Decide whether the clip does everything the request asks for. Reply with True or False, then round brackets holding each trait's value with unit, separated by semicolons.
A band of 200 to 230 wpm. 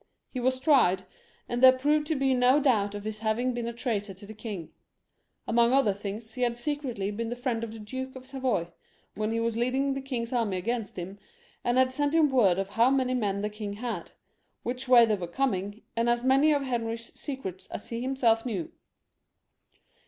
True (205 wpm)